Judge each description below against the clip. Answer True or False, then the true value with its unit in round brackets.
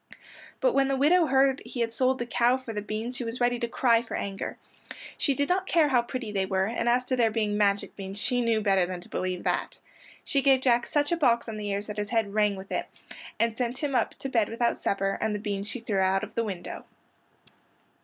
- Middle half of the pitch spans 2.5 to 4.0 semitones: True (3.7 semitones)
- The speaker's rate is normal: False (245 wpm)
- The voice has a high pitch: True (230 Hz)